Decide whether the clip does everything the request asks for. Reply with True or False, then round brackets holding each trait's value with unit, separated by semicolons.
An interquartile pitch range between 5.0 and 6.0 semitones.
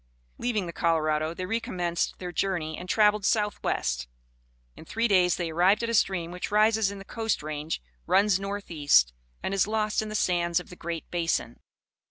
False (3.8 semitones)